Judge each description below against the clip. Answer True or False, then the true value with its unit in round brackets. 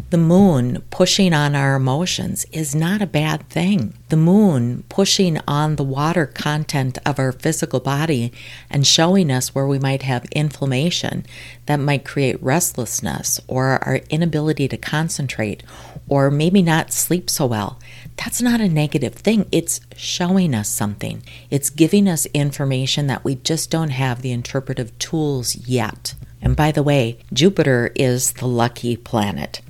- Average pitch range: True (4.1 semitones)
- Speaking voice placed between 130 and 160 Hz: True (140 Hz)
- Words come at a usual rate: True (155 wpm)